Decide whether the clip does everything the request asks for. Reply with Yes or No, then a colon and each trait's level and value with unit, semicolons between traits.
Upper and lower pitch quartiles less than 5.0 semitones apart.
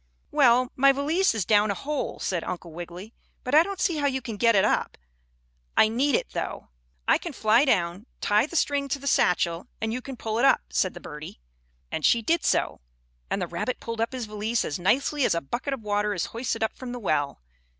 No: wide, 5.6 semitones